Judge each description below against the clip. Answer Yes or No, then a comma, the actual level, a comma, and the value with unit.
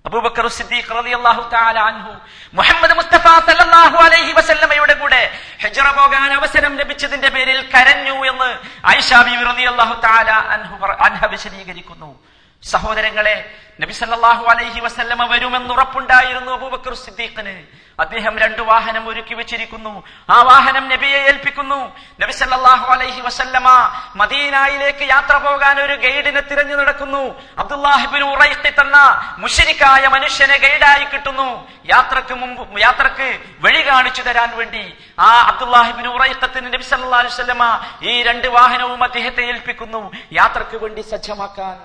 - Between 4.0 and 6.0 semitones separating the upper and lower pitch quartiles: No, average, 3.2 semitones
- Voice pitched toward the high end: Yes, very high, 255 Hz